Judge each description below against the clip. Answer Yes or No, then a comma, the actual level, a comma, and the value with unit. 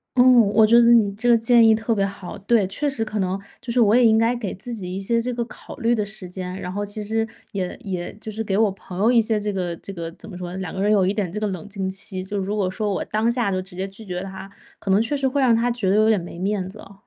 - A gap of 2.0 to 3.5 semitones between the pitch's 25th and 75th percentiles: Yes, average, 3.1 semitones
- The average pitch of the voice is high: Yes, high, 210 Hz